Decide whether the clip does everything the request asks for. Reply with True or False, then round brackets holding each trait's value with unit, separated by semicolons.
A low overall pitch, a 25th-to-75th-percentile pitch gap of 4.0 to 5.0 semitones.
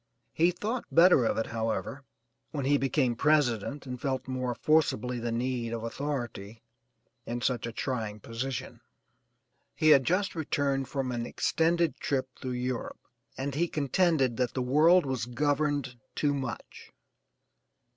False (130 Hz; 3.6 semitones)